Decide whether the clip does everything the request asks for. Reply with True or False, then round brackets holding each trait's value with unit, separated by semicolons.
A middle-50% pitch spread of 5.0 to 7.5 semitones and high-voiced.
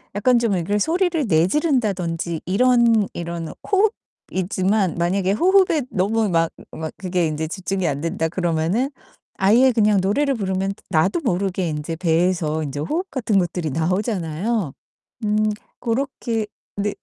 True (5.3 semitones; 195 Hz)